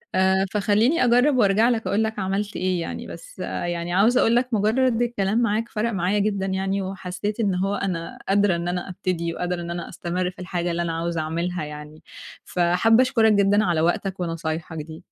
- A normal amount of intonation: Yes, average, 3.6 semitones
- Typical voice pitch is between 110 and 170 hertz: No, high, 190 Hz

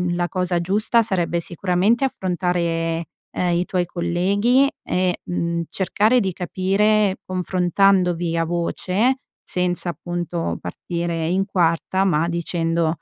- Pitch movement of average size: No, narrow, 2.1 semitones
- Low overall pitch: No, medium, 180 Hz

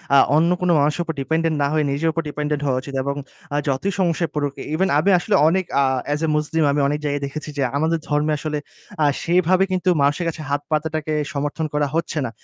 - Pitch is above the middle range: No, medium, 155 Hz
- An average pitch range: No, narrow, 2.3 semitones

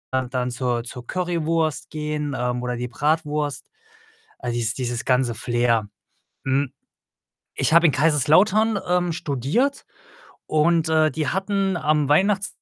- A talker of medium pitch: Yes, medium, 150 Hz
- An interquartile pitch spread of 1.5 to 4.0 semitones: No, average, 5.2 semitones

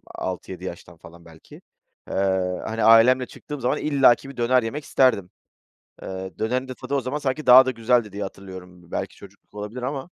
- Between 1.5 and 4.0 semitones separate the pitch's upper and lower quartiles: No, wide, 5.5 semitones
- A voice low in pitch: Yes, low, 115 Hz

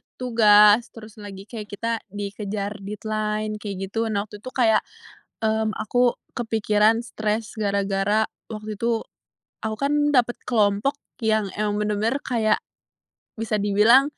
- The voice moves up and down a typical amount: No, narrow, 1.6 semitones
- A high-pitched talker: Yes, high, 215 Hz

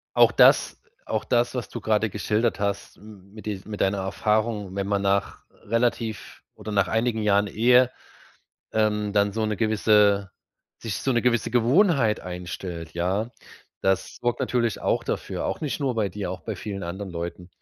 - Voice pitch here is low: Yes, low, 105 Hz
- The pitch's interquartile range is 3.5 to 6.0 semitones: No, average, 2.7 semitones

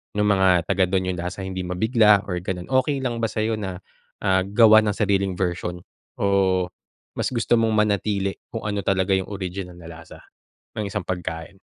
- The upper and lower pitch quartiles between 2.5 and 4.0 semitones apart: Yes, average, 2.8 semitones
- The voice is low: Yes, very low, 95 Hz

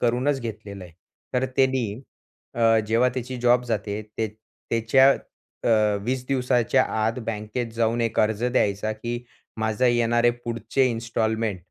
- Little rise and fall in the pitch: Yes, narrow, 2.1 semitones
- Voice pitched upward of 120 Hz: No, low, 115 Hz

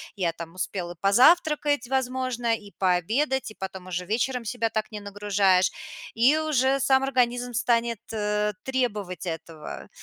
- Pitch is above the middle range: Yes, high, 225 Hz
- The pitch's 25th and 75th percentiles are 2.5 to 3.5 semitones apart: No, average, 5.0 semitones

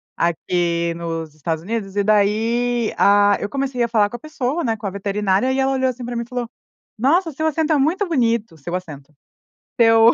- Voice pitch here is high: Yes, high, 225 Hz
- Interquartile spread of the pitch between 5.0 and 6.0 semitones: Yes, average, 5.3 semitones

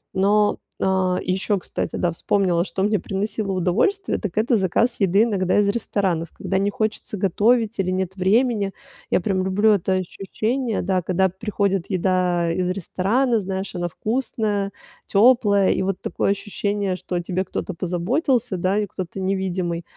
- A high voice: Yes, high, 195 Hz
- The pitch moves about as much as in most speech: No, narrow, 2.3 semitones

